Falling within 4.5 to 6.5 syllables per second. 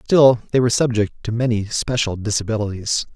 Yes: 5.9 syllables/s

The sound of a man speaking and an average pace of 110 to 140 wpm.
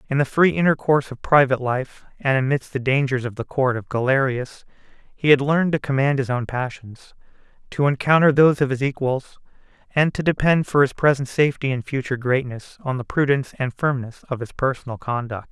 No: male; average, 190 wpm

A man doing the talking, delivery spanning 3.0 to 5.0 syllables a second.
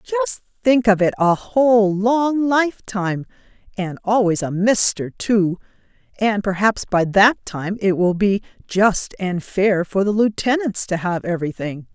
No: female; 4.6 syllables/s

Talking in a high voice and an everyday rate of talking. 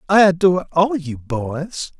No: medium, 165 Hz; average, 150 wpm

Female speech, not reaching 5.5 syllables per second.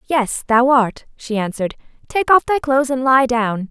Yes: female; 4.7 syllables/s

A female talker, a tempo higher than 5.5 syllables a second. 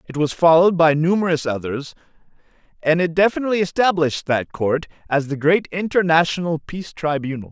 No: male; 5.9 syllables/s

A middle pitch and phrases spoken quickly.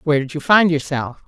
Yes: medium, 150 Hz; fast, 235 wpm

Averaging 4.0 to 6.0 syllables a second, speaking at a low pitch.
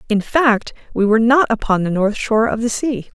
No: 5.4 syllables/s; high, 225 Hz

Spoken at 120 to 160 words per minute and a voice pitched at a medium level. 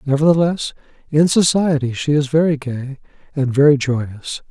Yes: slow, 135 wpm; medium, 145 Hz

